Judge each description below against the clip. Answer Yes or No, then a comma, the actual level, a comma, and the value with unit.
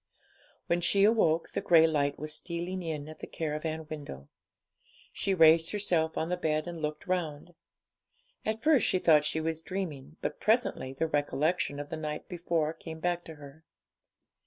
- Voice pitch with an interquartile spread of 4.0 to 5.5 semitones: No, narrow, 2.5 semitones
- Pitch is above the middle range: No, medium, 160 Hz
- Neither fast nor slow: Yes, average, 170 wpm